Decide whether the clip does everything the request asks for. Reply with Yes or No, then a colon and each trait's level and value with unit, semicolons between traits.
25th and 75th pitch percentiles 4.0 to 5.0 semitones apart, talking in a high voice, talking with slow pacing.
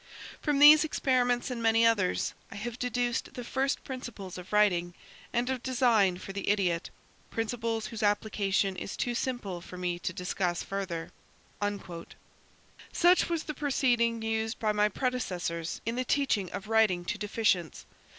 No: average, 4.5 semitones; high, 220 Hz; average, 150 wpm